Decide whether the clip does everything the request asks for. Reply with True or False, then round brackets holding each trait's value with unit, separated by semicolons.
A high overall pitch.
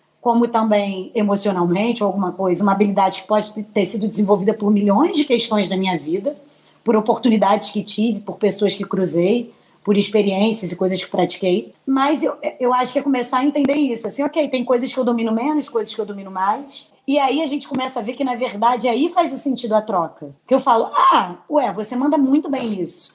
True (225 Hz)